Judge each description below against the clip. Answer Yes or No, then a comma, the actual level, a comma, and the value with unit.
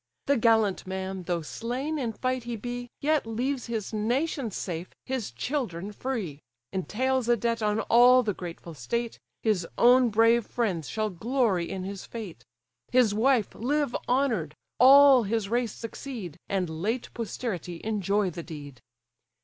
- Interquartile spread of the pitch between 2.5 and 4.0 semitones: No, average, 4.8 semitones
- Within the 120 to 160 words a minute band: Yes, average, 150 wpm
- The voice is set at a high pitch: Yes, high, 225 Hz